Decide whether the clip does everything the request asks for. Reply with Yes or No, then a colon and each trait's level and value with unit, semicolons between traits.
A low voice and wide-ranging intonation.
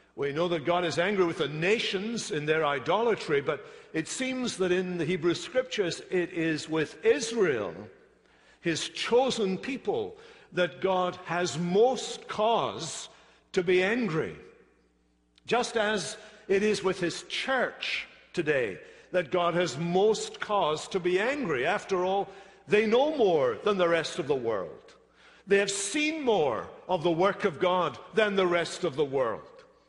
No: high, 190 Hz; wide, 6.7 semitones